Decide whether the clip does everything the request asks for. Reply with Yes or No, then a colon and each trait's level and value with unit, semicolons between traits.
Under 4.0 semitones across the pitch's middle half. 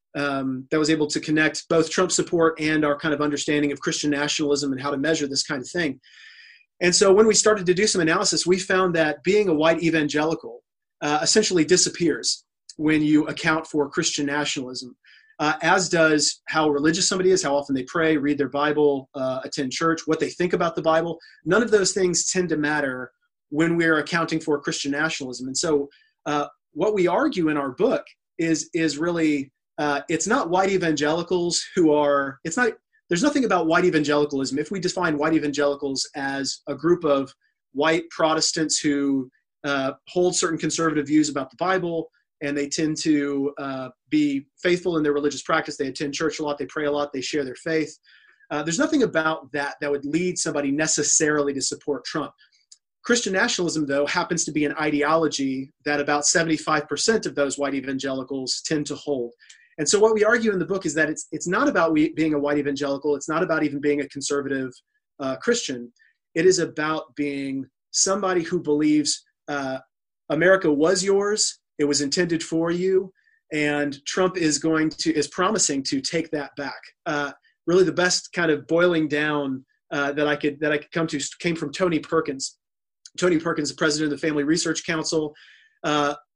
Yes: average, 3.3 semitones